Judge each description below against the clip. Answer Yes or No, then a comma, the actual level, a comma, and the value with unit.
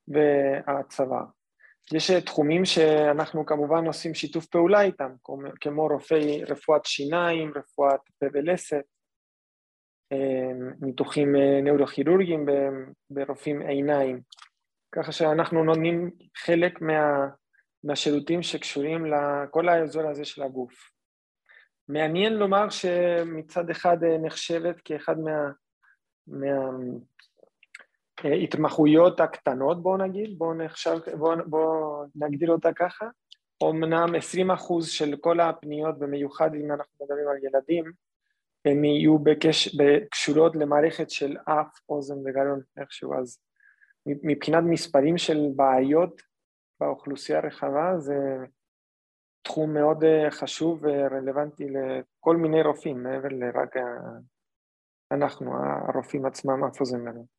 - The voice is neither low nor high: Yes, medium, 150 Hz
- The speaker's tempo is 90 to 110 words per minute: Yes, slow, 100 wpm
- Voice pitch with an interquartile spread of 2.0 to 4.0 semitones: Yes, average, 2.9 semitones